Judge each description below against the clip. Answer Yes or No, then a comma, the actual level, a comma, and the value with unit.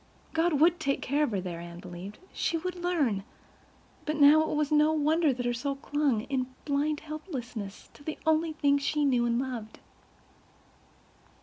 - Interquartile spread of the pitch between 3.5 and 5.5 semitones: Yes, average, 4.3 semitones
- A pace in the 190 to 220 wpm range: No, average, 150 wpm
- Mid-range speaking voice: No, very high, 285 Hz